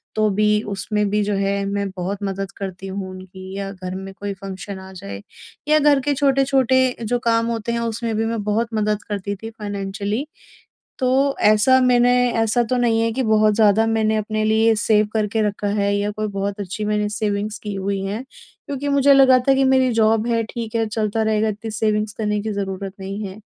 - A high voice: Yes, high, 215 Hz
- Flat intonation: Yes, narrow, 2.3 semitones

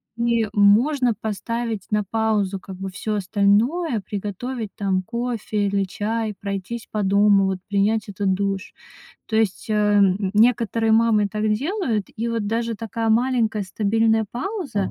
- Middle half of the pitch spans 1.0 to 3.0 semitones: Yes, narrow, 2.4 semitones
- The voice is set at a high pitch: Yes, high, 215 Hz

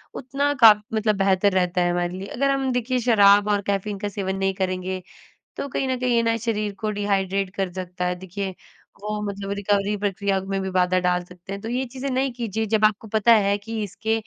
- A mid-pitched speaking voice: No, high, 200 Hz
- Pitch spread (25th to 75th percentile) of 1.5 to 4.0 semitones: Yes, average, 2.8 semitones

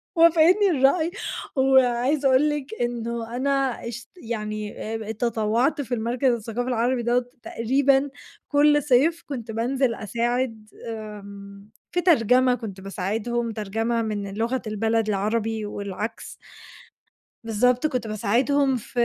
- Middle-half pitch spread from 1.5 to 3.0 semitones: No, average, 3.4 semitones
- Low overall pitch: No, high, 235 Hz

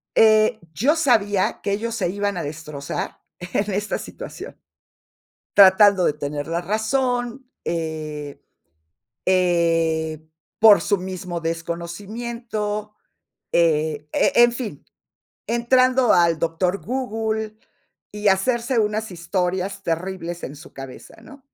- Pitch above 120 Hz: Yes, high, 190 Hz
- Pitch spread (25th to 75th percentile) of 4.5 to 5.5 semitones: Yes, average, 4.8 semitones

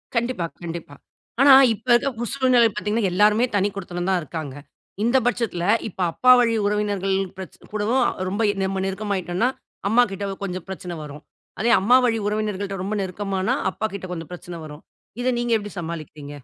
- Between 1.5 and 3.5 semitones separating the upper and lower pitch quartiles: No, average, 4.1 semitones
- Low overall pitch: No, high, 200 Hz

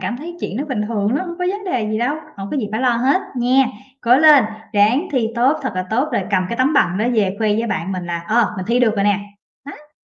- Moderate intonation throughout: Yes, average, 4.7 semitones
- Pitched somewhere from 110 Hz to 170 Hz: No, high, 235 Hz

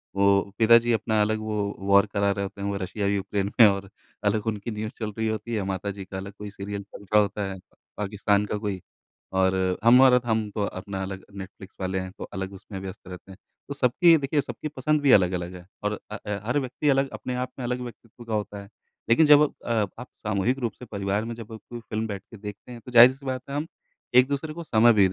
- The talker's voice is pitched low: Yes, low, 105 Hz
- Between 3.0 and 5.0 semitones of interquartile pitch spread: Yes, average, 3.5 semitones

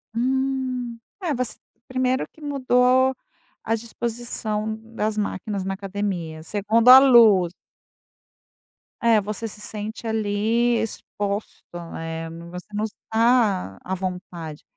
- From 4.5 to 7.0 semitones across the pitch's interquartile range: No, average, 3.7 semitones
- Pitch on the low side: No, high, 220 Hz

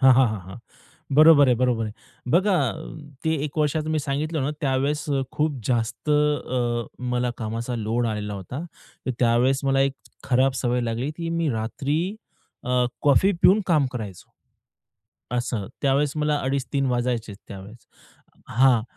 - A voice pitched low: Yes, low, 130 Hz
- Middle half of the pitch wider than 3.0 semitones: Yes, average, 3.9 semitones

